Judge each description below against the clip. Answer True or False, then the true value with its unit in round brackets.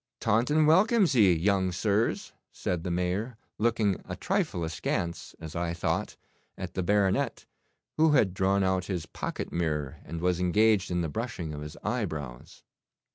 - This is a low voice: True (95 Hz)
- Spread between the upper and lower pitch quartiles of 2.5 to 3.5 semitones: False (4.5 semitones)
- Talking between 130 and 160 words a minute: True (155 wpm)